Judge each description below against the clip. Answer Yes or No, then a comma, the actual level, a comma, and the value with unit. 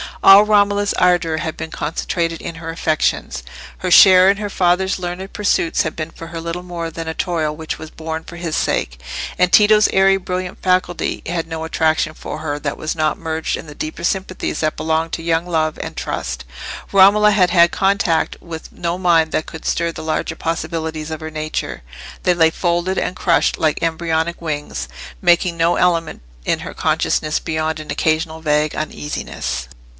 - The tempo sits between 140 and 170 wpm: No, average, 180 wpm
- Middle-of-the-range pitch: Yes, medium, 165 Hz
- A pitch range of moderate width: No, narrow, 2.2 semitones